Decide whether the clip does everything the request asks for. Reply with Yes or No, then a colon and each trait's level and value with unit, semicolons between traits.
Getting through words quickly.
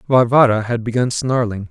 No: average, 140 wpm